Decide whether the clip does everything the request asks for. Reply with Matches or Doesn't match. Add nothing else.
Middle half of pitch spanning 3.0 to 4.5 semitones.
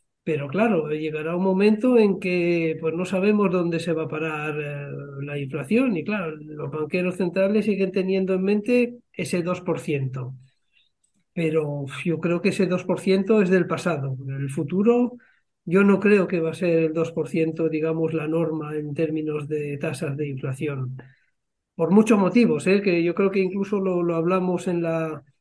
Matches